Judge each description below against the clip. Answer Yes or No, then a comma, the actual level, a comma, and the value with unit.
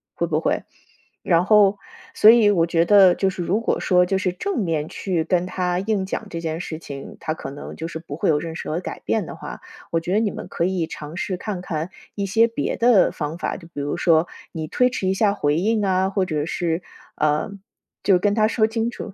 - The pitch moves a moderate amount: Yes, average, 3.7 semitones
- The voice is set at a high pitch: No, medium, 180 Hz